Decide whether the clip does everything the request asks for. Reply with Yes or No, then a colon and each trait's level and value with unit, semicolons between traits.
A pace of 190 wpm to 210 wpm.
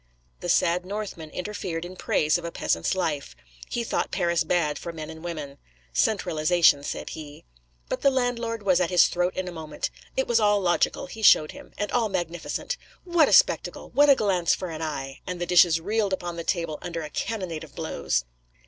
Yes: average, 200 wpm